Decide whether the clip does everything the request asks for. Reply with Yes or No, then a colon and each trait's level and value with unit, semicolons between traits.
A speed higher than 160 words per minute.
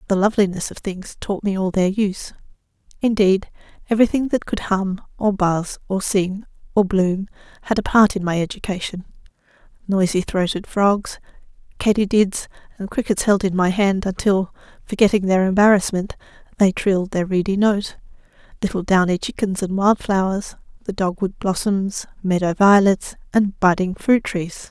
No: average, 145 wpm